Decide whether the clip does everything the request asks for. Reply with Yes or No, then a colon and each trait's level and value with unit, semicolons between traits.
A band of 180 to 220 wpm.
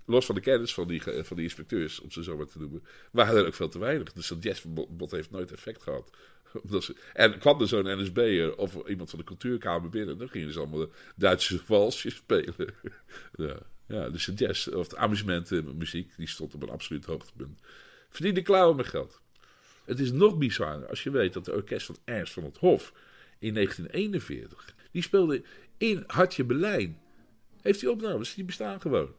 Yes: average, 195 wpm